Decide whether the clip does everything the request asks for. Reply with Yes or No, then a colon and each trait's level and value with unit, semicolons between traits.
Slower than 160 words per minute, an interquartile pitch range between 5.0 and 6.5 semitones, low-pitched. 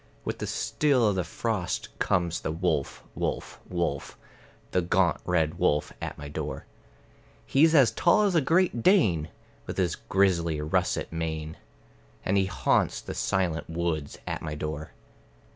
Yes: average, 150 wpm; wide, 5.6 semitones; very low, 85 Hz